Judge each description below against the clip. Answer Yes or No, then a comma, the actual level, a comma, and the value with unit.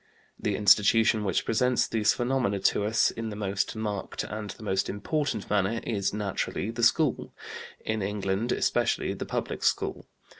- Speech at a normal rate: Yes, average, 155 wpm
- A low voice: Yes, low, 105 Hz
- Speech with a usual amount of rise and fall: No, narrow, 2.3 semitones